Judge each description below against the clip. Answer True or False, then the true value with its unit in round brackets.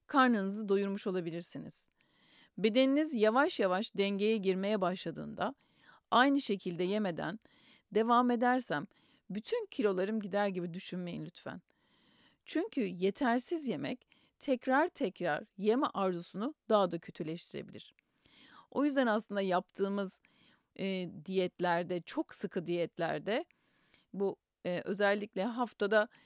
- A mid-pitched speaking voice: False (205 Hz)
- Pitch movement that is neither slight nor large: True (4.7 semitones)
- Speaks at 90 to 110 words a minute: True (100 wpm)